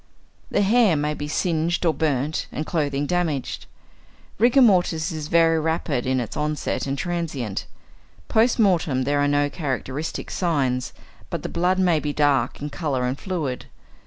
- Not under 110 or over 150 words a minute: No, average, 160 wpm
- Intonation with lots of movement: No, average, 3.7 semitones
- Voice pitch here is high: No, medium, 155 Hz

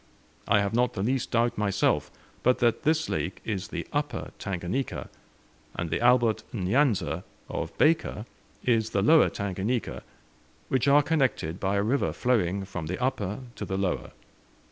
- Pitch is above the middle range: No, low, 110 Hz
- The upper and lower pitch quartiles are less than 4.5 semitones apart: No, average, 4.8 semitones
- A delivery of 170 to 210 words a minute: No, average, 155 wpm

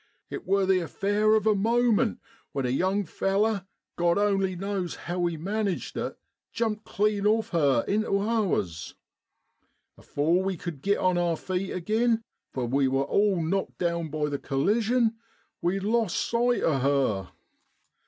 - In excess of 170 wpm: No, average, 155 wpm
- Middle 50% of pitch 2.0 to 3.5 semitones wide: No, average, 4.3 semitones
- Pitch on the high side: Yes, high, 195 Hz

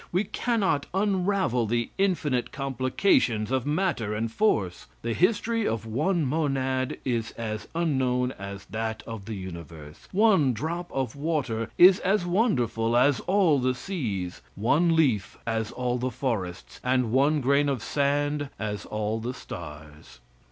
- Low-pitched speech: Yes, low, 130 Hz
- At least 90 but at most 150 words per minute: Yes, average, 145 wpm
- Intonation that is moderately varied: No, wide, 6.3 semitones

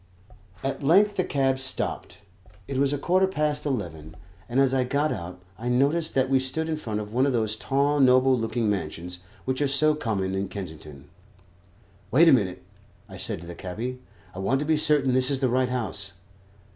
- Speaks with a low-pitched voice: Yes, low, 130 Hz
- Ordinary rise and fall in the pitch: No, wide, 6.1 semitones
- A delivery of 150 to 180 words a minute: No, average, 195 wpm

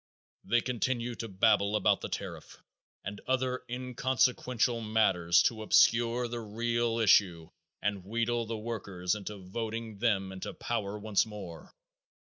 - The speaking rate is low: Yes, slow, 130 wpm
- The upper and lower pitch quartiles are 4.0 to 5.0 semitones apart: No, average, 2.9 semitones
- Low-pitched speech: Yes, low, 110 Hz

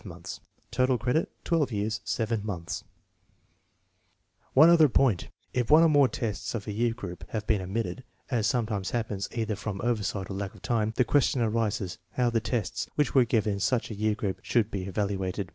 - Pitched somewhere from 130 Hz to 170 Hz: No, low, 110 Hz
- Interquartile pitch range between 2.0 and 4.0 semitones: Yes, average, 3.3 semitones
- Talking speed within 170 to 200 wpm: Yes, average, 180 wpm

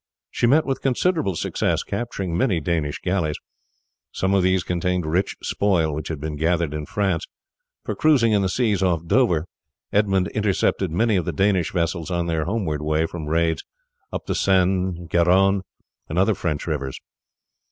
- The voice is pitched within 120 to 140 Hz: No, very low, 90 Hz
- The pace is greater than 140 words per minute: Yes, average, 165 wpm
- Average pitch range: Yes, average, 3.3 semitones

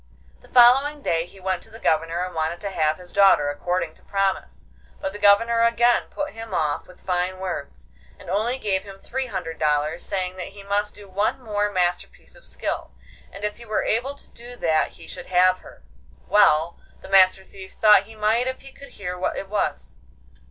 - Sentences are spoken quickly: Yes, fast, 210 wpm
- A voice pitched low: No, high, 195 Hz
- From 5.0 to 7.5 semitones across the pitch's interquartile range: No, average, 3.7 semitones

